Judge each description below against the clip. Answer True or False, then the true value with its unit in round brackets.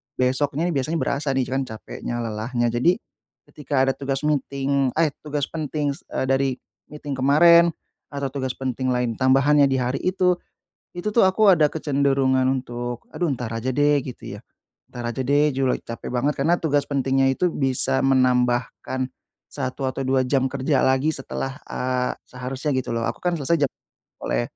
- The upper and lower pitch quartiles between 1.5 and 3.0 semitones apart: True (2.4 semitones)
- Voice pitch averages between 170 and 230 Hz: False (135 Hz)